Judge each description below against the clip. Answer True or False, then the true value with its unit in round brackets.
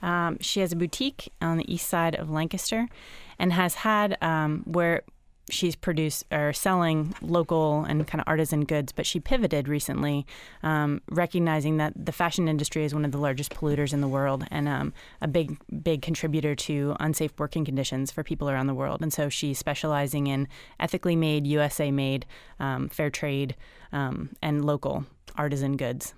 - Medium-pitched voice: True (155 Hz)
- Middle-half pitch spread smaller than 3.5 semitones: True (2.7 semitones)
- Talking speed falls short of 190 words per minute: True (175 wpm)